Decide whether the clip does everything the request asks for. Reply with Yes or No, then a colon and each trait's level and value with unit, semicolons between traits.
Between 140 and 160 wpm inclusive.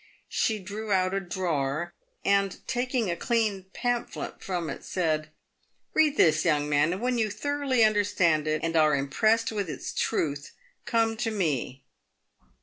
Yes: average, 155 wpm